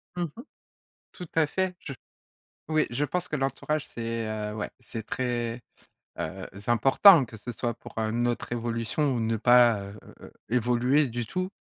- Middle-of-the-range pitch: No, low, 120 Hz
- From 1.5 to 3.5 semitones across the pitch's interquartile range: No, average, 4.2 semitones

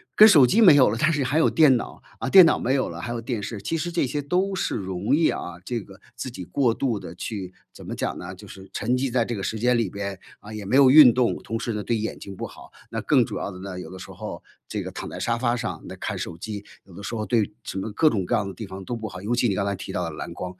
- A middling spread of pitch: Yes, average, 4.8 semitones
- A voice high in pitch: No, low, 115 Hz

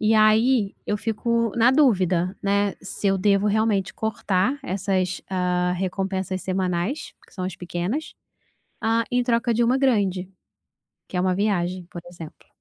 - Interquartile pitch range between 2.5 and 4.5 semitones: Yes, average, 3.6 semitones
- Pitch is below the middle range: No, high, 200 Hz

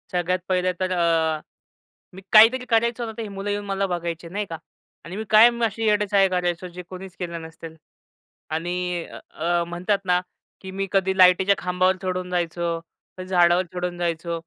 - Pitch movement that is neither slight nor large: No, narrow, 2.2 semitones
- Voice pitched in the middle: Yes, medium, 180 Hz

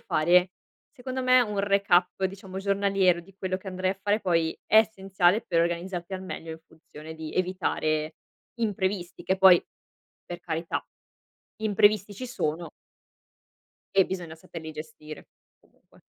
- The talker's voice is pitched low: No, medium, 185 Hz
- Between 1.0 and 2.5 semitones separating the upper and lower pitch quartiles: No, average, 2.9 semitones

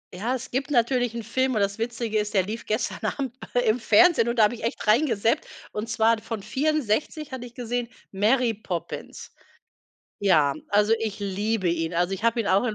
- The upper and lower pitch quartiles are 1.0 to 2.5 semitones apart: No, average, 2.9 semitones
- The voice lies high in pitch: Yes, high, 225 Hz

